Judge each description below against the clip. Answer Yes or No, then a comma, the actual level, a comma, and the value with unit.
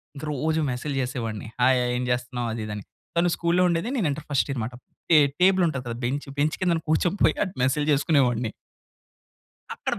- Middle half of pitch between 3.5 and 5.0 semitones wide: Yes, average, 4.4 semitones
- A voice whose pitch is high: No, medium, 140 Hz